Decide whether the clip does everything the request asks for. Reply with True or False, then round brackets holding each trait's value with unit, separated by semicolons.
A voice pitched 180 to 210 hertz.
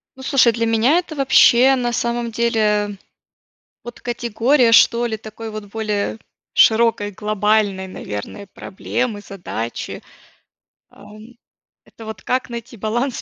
False (225 Hz)